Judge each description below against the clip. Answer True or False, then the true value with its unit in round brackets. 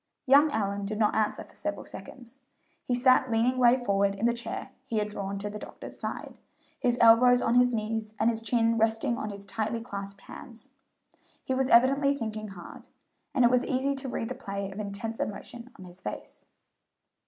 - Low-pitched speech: False (225 Hz)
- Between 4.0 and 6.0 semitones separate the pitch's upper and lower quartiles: False (3.1 semitones)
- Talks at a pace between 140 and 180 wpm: False (195 wpm)